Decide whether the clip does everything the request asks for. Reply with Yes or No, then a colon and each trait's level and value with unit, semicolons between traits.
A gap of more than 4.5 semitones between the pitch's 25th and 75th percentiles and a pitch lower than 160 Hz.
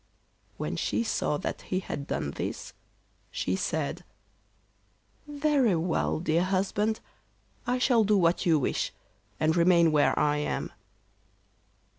No: wide, 5.4 semitones; medium, 175 Hz